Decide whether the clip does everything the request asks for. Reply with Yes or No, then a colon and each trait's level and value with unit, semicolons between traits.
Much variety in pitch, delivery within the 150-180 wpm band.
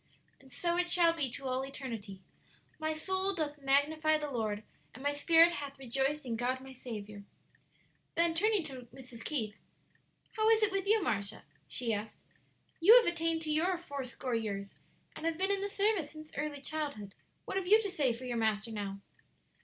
No: wide, 6.0 semitones; average, 190 wpm